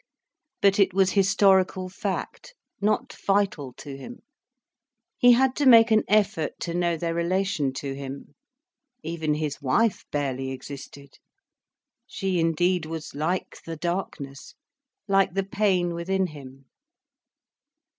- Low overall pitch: No, medium, 175 Hz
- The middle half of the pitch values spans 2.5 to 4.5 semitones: No, average, 4.9 semitones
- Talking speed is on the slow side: Yes, slow, 125 wpm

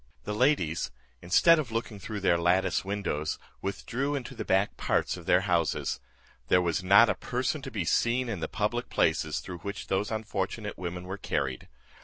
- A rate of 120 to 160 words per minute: No, average, 180 wpm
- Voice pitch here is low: Yes, low, 100 Hz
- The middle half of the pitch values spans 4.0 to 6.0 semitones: Yes, average, 4.7 semitones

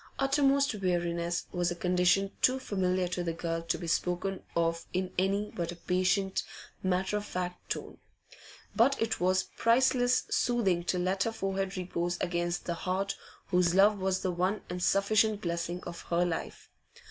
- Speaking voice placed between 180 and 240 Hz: Yes, medium, 185 Hz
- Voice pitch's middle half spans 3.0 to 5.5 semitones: No, narrow, 2.4 semitones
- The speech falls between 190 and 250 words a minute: No, average, 165 wpm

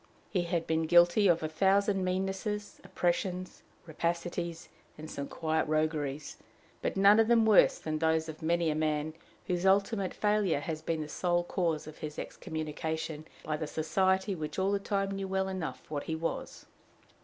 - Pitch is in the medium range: Yes, medium, 170 Hz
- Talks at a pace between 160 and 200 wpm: Yes, average, 170 wpm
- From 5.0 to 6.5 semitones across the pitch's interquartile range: No, average, 3.4 semitones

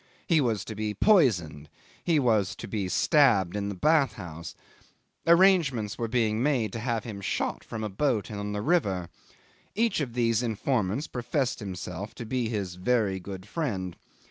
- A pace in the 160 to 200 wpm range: Yes, average, 170 wpm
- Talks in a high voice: No, low, 110 Hz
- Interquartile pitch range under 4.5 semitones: No, average, 5.1 semitones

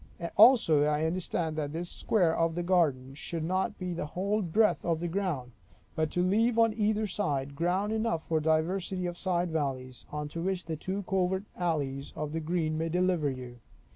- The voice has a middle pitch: Yes, medium, 170 Hz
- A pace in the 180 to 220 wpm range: Yes, average, 185 wpm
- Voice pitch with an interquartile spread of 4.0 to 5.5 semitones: No, average, 3.5 semitones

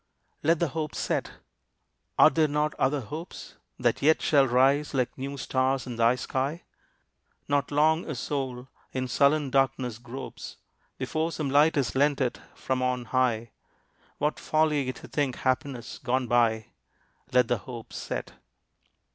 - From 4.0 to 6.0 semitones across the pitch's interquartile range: No, average, 2.9 semitones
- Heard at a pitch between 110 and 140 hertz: Yes, low, 135 Hz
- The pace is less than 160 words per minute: Yes, average, 145 wpm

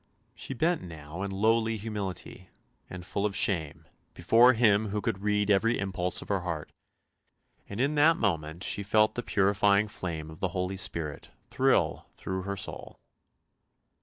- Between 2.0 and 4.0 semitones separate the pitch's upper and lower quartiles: Yes, average, 3.0 semitones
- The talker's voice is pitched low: Yes, low, 100 Hz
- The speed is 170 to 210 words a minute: No, average, 160 wpm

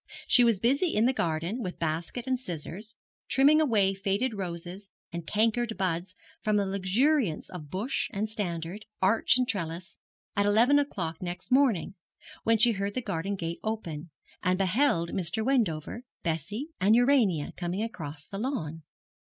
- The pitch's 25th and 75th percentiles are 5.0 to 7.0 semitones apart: Yes, average, 5.3 semitones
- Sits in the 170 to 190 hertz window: No, high, 200 Hz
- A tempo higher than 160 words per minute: No, average, 155 wpm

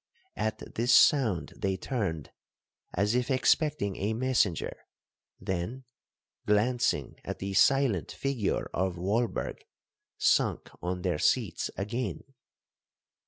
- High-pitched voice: No, low, 105 Hz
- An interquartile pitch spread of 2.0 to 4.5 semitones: No, average, 5.0 semitones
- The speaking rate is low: Yes, slow, 105 wpm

